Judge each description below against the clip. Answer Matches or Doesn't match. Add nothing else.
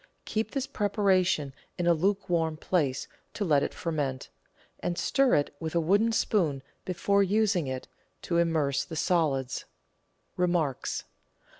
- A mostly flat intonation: Doesn't match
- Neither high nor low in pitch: Matches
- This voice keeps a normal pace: Matches